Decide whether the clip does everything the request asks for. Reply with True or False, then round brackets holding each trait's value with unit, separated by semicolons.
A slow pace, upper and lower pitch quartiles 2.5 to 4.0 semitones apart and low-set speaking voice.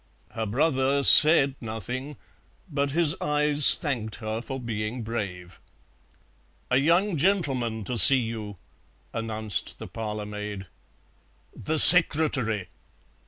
False (110 wpm; 5.2 semitones; 125 Hz)